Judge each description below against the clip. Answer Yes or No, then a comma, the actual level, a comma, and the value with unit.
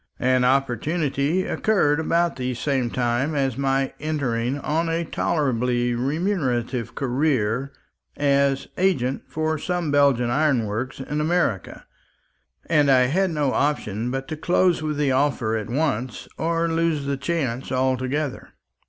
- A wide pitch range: No, average, 3.7 semitones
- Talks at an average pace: No, slow, 130 wpm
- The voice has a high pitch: No, medium, 140 Hz